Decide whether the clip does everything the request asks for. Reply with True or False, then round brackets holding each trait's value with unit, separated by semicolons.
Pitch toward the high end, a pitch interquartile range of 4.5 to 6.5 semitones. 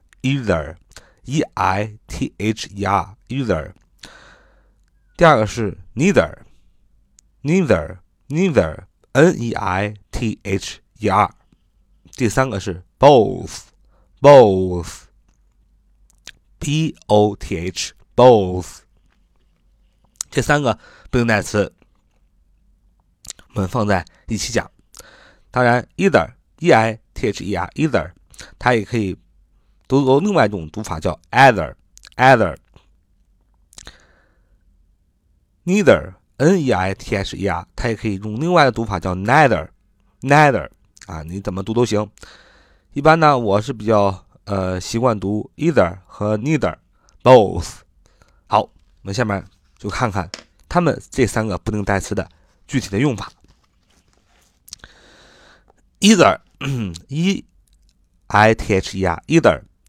False (100 Hz; 5.2 semitones)